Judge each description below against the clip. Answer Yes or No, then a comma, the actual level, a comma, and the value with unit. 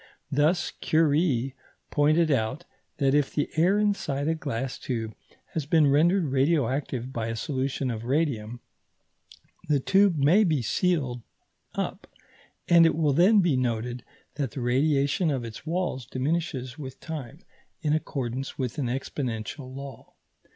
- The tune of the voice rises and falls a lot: No, average, 3.9 semitones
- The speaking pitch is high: No, medium, 140 Hz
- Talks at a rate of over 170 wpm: No, average, 140 wpm